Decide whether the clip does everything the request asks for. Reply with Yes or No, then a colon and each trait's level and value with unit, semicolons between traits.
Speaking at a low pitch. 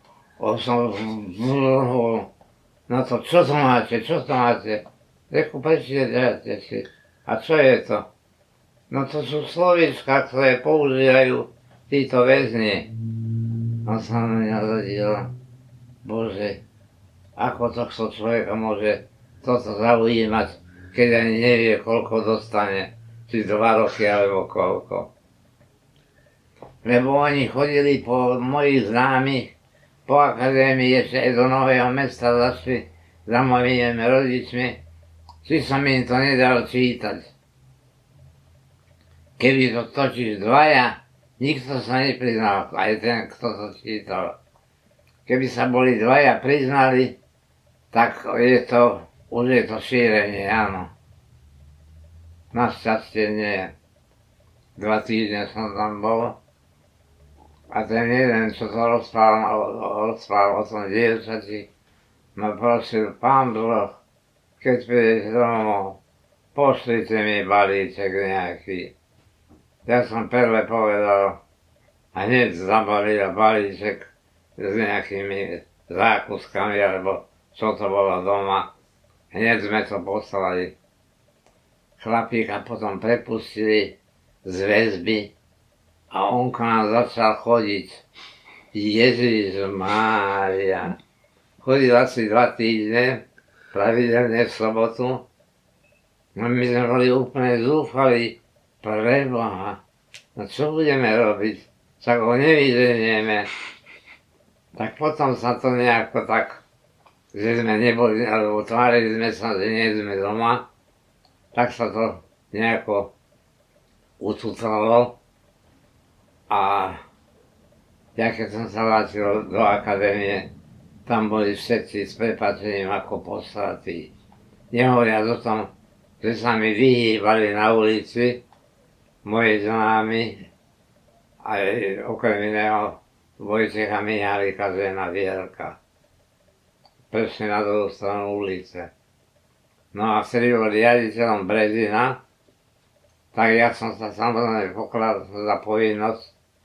Yes: low, 110 Hz